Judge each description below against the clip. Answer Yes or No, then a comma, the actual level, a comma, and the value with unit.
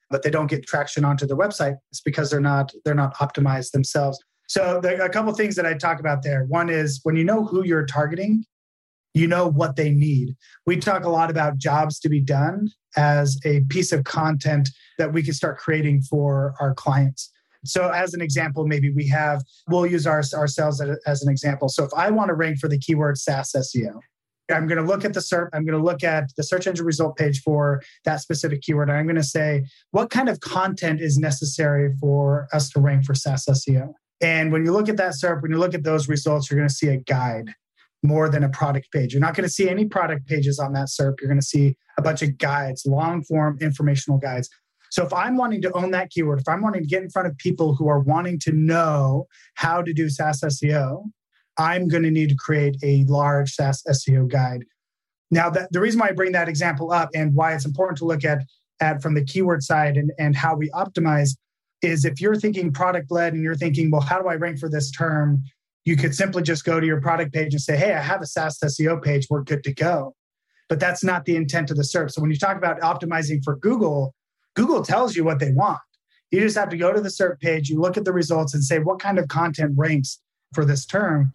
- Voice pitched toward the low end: No, medium, 155 Hz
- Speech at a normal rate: No, fast, 240 wpm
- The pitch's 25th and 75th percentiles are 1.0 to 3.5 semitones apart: Yes, average, 3.1 semitones